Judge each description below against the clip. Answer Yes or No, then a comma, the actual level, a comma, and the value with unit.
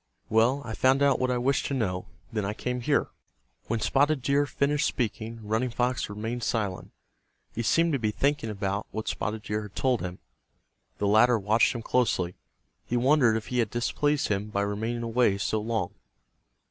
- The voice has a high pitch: No, low, 115 Hz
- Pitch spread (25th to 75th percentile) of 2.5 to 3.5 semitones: Yes, average, 3.2 semitones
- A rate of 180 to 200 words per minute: Yes, average, 185 wpm